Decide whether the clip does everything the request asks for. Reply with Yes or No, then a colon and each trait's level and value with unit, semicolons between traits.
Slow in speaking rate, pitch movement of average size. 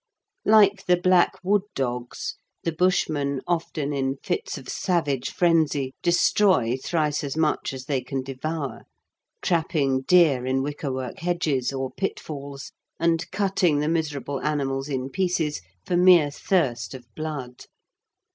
Yes: slow, 130 wpm; average, 4.4 semitones